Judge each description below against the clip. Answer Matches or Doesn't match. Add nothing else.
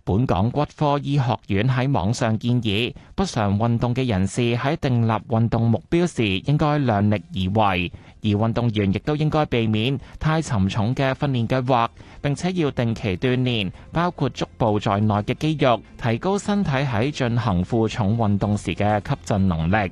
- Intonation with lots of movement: Doesn't match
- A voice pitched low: Matches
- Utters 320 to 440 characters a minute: Doesn't match